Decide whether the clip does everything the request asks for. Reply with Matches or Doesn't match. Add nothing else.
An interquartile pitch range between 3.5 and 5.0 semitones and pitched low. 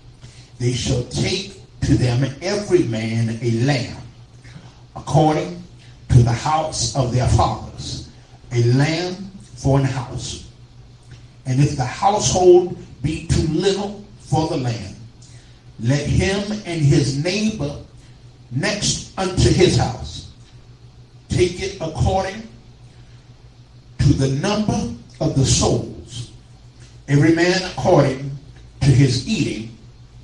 Matches